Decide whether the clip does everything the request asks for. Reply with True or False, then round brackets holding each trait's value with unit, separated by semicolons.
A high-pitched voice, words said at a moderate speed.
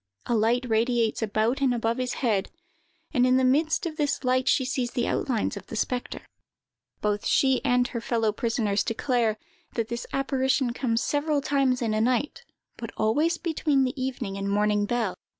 True (245 Hz; 180 wpm)